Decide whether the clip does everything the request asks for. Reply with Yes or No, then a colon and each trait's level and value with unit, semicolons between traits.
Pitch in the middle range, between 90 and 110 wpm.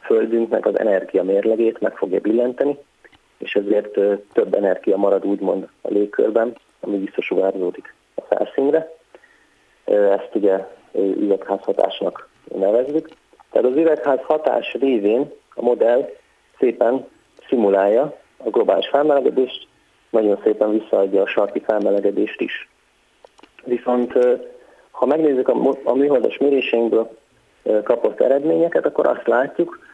Yes: medium, 150 Hz; slow, 105 wpm